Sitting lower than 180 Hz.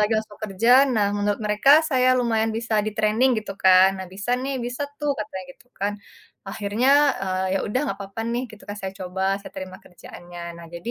No: high, 210 Hz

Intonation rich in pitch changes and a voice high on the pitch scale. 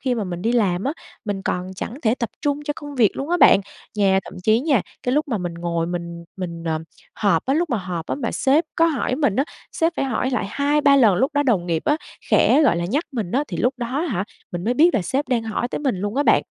Yes: wide, 7.5 semitones; high, 235 Hz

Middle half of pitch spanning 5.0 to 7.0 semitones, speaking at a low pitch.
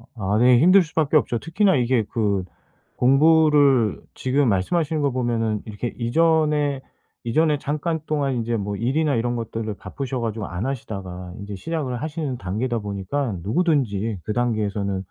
Yes: wide, 5.6 semitones; low, 120 Hz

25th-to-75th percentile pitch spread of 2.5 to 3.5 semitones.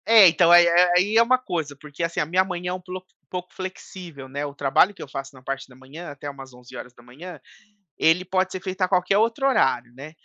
No: average, 5.0 semitones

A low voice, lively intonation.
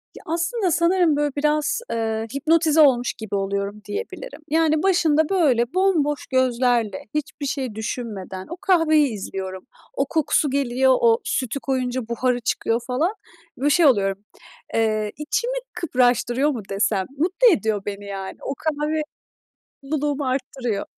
No: very high, 270 Hz; wide, 5.7 semitones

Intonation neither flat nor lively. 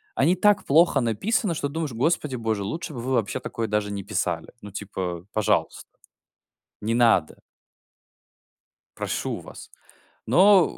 No: wide, 8.0 semitones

